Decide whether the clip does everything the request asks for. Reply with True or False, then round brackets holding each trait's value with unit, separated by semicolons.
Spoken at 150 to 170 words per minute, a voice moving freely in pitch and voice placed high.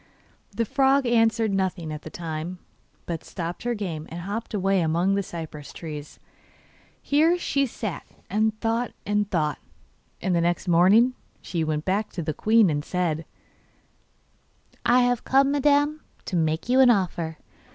True (155 wpm; 6.1 semitones; 195 Hz)